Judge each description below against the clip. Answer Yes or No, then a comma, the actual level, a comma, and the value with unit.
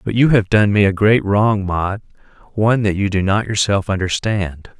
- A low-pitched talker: Yes, low, 100 Hz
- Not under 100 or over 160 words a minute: No, average, 200 wpm